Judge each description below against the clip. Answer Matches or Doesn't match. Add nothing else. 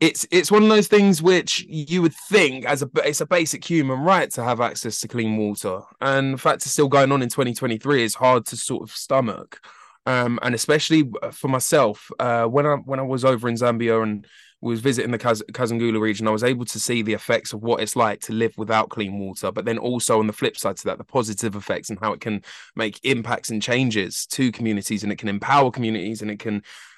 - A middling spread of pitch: Matches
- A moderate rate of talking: Doesn't match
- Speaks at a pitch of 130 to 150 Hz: Doesn't match